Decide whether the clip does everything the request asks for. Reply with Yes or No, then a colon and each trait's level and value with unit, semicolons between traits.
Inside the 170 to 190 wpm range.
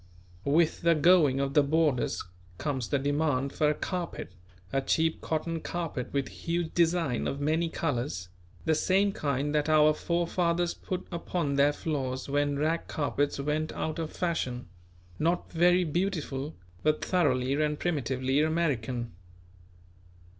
No: average, 140 wpm